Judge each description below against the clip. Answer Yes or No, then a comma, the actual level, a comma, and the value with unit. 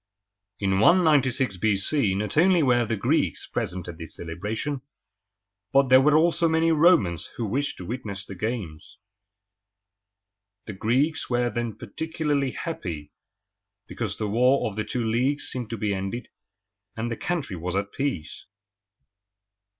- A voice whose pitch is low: Yes, low, 120 Hz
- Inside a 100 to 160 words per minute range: Yes, average, 140 wpm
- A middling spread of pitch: No, wide, 6.3 semitones